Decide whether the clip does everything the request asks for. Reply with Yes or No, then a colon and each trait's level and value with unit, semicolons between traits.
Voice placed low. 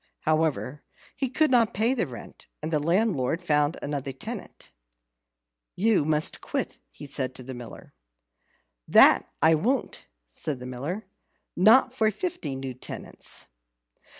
No: medium, 155 Hz